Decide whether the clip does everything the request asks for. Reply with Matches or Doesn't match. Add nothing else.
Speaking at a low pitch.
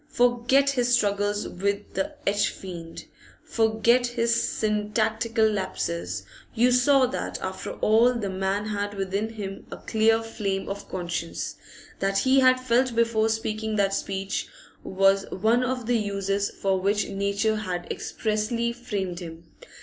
Doesn't match